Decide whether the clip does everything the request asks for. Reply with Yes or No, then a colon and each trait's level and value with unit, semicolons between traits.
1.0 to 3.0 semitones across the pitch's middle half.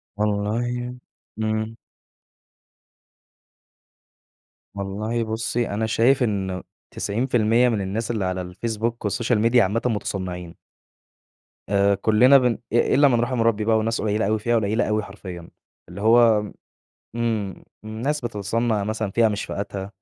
Yes: narrow, 2.5 semitones